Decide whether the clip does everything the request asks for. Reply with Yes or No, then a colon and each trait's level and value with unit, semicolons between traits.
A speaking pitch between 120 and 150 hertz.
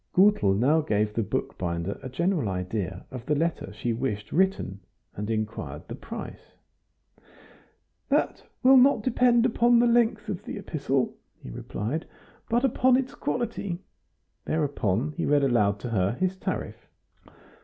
Yes: medium, 140 Hz